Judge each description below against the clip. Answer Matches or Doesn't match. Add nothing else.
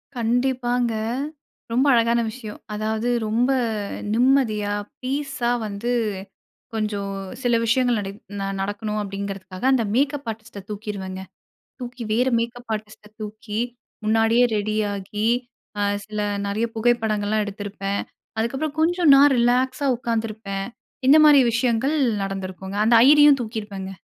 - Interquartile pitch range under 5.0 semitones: Matches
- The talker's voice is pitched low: Doesn't match